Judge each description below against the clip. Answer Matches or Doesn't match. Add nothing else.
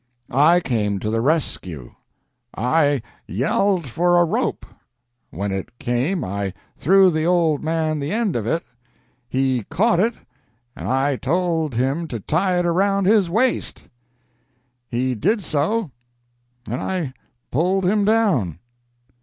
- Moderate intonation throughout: Doesn't match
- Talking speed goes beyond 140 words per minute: Doesn't match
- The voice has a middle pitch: Matches